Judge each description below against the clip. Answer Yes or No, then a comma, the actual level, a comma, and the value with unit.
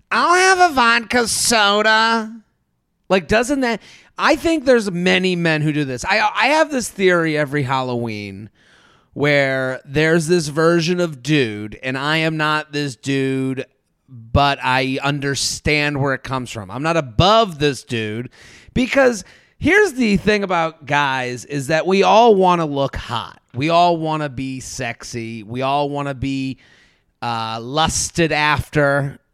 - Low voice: No, medium, 150 Hz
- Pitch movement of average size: No, wide, 6.2 semitones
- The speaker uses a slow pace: No, average, 155 wpm